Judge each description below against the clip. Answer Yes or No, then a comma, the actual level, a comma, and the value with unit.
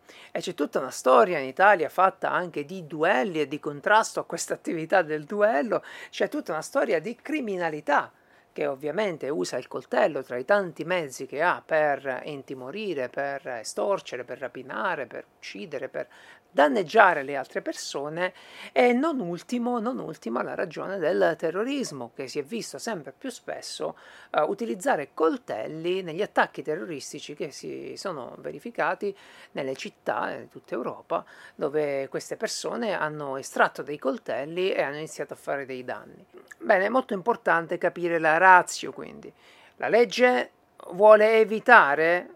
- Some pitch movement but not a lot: No, wide, 6.8 semitones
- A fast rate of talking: No, average, 150 wpm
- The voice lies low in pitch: No, medium, 180 Hz